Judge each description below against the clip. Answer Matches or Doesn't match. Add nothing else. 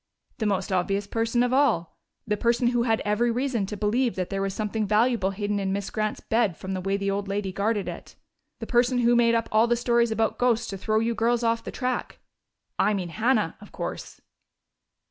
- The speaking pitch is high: Matches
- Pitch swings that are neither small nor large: Matches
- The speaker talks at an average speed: Doesn't match